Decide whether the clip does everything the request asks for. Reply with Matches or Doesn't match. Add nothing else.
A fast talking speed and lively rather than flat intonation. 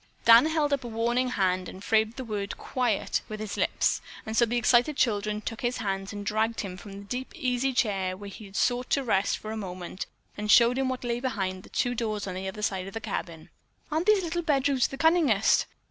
Doesn't match